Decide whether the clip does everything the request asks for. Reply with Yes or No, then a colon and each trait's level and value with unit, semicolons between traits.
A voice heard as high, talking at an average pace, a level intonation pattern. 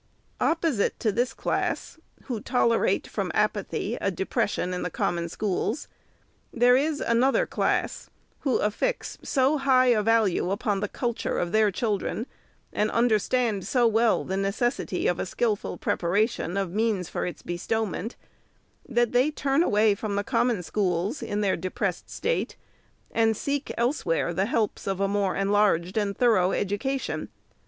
No: high, 215 Hz; average, 155 wpm; average, 3.9 semitones